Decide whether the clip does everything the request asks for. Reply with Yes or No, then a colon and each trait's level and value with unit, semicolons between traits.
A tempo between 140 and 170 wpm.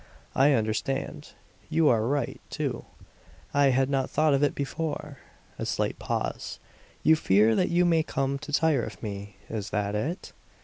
Yes: average, 165 wpm